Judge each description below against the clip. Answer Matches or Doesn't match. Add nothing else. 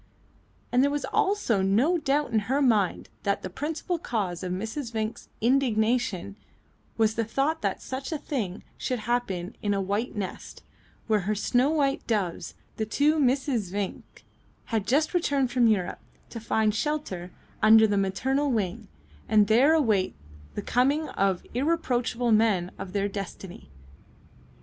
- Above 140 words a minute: Matches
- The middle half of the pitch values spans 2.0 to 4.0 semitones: Doesn't match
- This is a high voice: Matches